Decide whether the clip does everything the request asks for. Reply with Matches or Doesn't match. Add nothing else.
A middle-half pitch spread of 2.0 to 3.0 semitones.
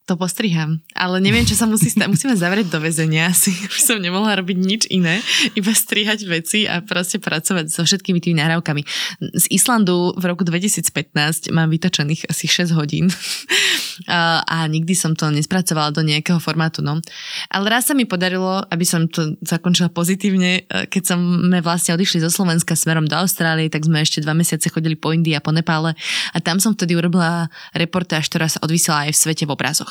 Matches